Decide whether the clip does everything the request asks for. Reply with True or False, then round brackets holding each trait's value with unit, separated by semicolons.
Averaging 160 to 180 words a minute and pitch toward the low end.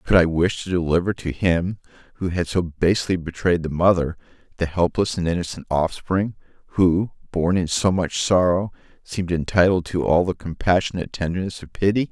True (170 wpm; 90 Hz)